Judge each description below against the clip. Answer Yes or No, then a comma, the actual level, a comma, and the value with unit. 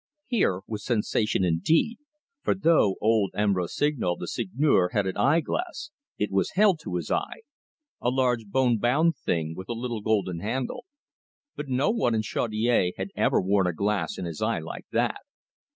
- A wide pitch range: Yes, wide, 6.2 semitones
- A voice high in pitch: No, low, 110 Hz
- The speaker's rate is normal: Yes, average, 175 wpm